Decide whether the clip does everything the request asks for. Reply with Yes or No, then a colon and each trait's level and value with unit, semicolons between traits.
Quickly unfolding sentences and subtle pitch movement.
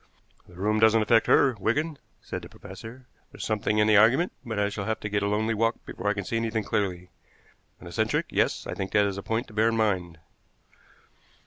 Yes: fast, 220 wpm; narrow, 1.9 semitones